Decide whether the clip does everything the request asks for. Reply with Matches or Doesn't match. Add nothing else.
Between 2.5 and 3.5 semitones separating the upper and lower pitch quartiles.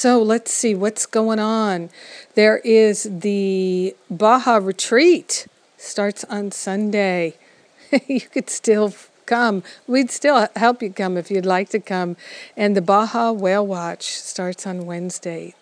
Matches